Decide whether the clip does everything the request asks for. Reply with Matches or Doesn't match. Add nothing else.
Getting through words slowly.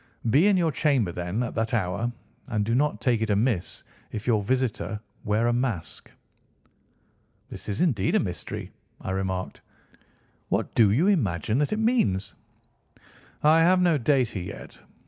Doesn't match